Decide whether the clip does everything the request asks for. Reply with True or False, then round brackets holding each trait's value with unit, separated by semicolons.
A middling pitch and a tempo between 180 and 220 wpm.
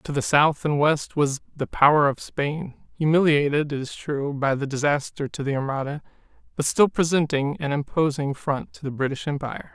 True (145 Hz; 185 wpm)